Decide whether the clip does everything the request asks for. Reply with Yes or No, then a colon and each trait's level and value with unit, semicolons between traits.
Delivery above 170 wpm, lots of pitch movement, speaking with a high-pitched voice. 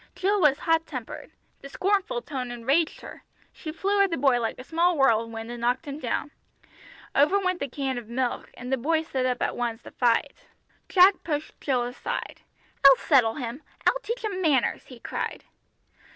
Yes: average, 185 wpm; wide, 5.7 semitones; very high, 275 Hz